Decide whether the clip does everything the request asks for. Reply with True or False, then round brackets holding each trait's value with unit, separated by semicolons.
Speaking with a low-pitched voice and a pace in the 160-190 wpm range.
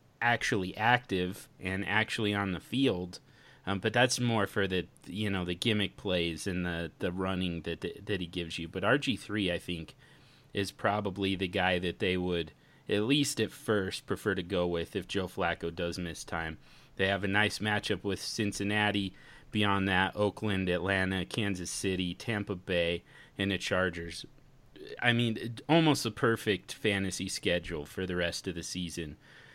True (95 Hz; 170 wpm)